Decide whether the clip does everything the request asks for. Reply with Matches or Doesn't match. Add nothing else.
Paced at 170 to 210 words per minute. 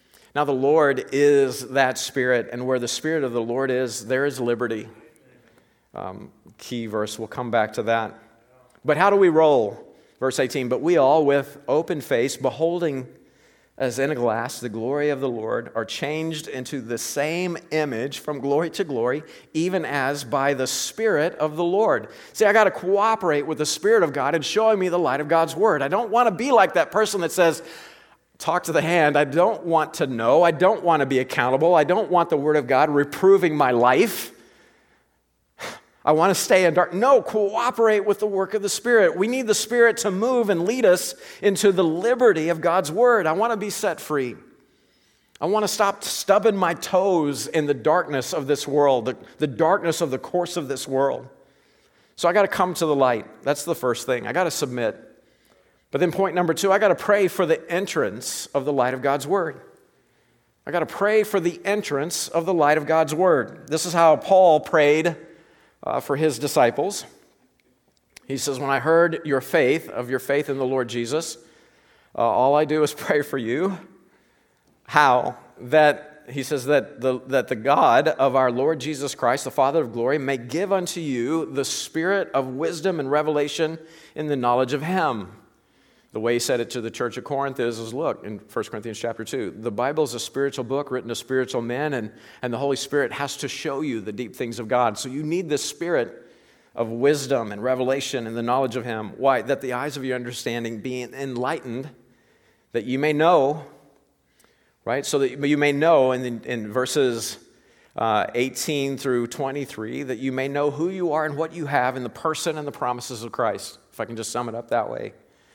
Matches